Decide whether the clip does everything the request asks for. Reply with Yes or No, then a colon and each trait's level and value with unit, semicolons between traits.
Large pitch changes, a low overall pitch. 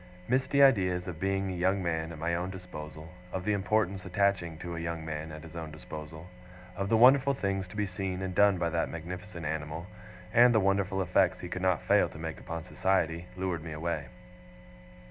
No: average, 3.1 semitones; very low, 90 Hz